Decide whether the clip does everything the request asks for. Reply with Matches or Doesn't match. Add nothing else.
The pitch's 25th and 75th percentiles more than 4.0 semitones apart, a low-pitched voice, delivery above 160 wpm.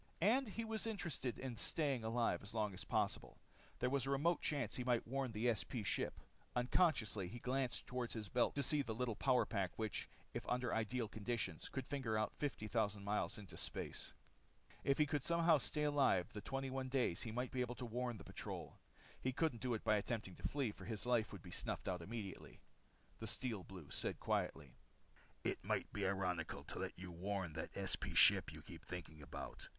Matches